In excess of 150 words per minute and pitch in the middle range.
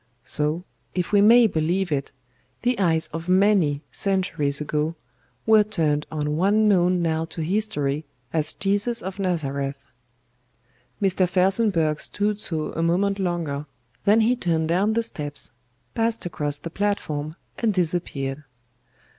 No: slow, 135 wpm; medium, 175 Hz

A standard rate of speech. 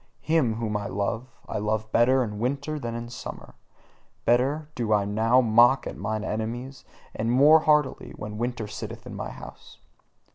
Yes: average, 170 wpm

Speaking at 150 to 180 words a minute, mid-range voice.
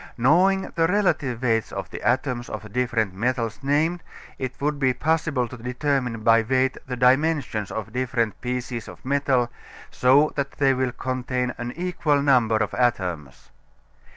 No: average, 155 wpm; low, 125 Hz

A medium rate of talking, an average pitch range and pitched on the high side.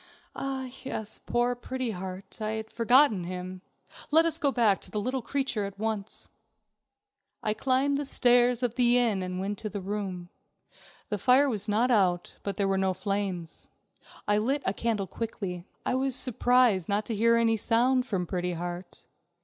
Yes: average, 180 wpm; average, 4.4 semitones; high, 220 Hz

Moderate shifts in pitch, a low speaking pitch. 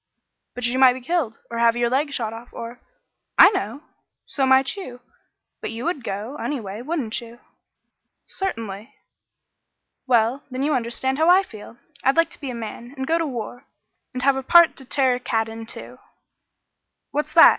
No: average, 3.5 semitones; very high, 255 Hz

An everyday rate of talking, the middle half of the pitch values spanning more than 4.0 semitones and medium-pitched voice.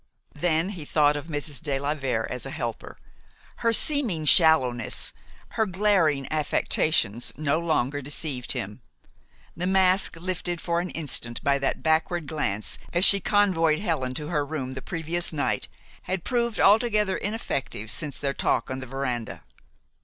Yes: average, 155 wpm; average, 4.8 semitones; medium, 155 Hz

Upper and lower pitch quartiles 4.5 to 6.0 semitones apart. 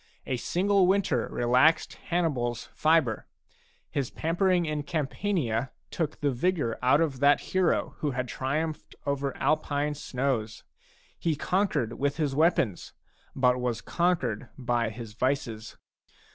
Yes: average, 4.8 semitones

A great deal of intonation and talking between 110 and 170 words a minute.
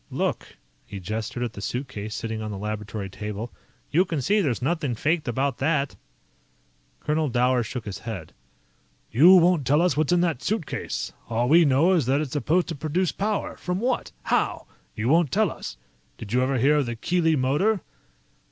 No: wide, 6.5 semitones; average, 185 wpm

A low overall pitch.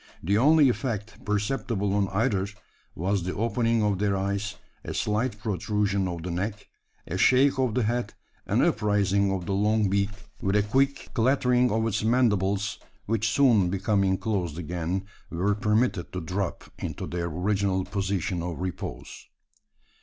Yes: low, 100 Hz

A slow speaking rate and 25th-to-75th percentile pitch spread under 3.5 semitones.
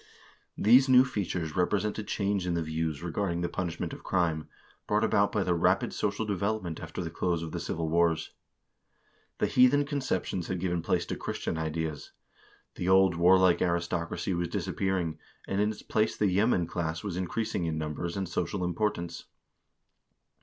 No: average, 165 wpm; average, 3.1 semitones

